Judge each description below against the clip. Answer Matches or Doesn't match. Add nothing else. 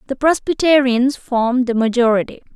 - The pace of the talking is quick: Doesn't match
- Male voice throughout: Doesn't match